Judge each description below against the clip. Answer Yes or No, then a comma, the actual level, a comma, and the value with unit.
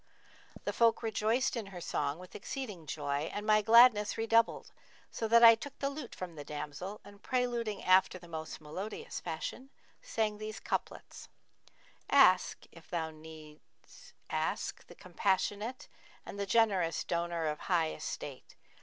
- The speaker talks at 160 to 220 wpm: No, average, 150 wpm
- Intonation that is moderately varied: No, wide, 5.8 semitones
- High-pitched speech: Yes, high, 200 Hz